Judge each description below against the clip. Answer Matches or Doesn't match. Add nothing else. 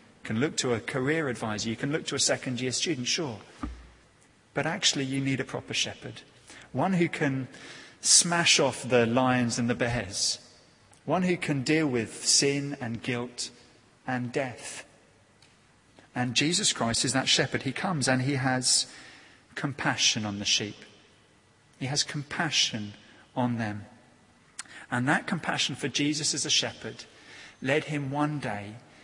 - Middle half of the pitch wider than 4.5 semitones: Doesn't match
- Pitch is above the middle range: Doesn't match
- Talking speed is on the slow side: Doesn't match